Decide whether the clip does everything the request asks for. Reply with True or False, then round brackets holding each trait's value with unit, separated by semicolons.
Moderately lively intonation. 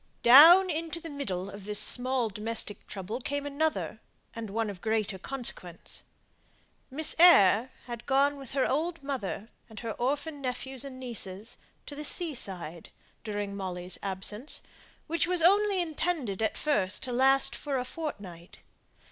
False (6.0 semitones)